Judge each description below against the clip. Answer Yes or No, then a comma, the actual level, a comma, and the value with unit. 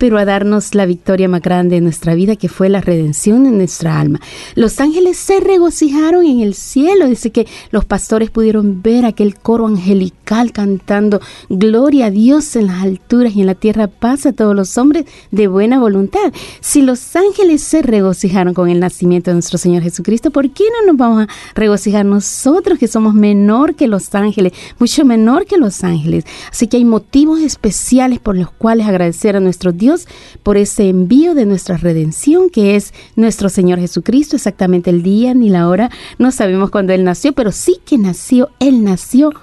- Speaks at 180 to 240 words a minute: Yes, average, 185 wpm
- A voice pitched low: No, high, 210 Hz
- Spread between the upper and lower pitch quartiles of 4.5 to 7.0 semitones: Yes, wide, 5.5 semitones